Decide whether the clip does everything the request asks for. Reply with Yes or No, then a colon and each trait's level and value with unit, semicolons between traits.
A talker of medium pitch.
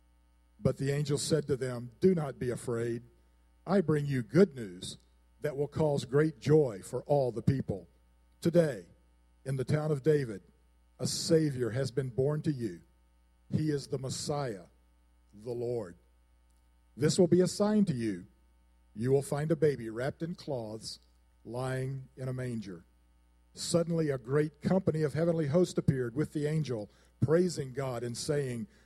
No: low, 130 Hz